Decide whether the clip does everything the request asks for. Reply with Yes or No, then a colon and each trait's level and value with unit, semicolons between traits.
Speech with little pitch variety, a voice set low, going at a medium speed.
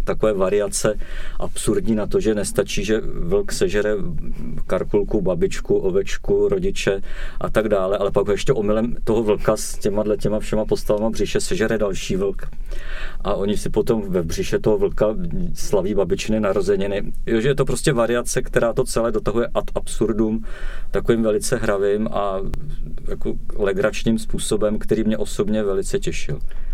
No: wide, 7.5 semitones; low, 110 Hz; average, 150 wpm